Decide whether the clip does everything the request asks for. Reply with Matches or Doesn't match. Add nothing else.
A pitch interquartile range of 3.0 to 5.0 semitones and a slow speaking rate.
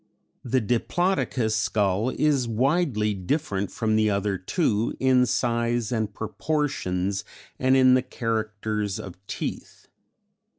Matches